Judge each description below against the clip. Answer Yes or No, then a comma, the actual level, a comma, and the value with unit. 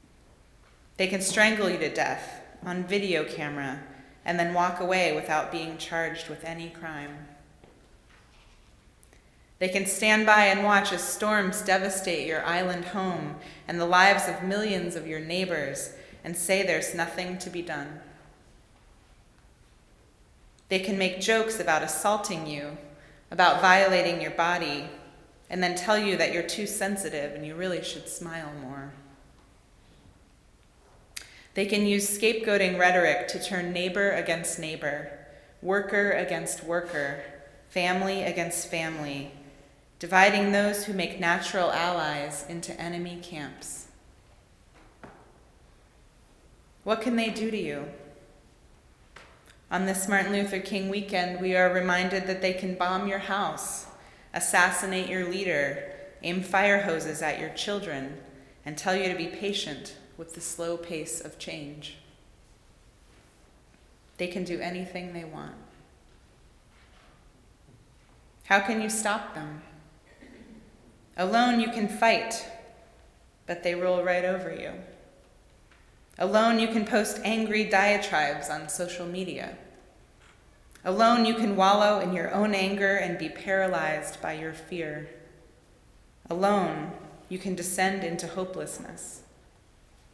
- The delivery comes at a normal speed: No, slow, 125 wpm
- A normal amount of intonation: Yes, average, 3.7 semitones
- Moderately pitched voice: Yes, medium, 180 Hz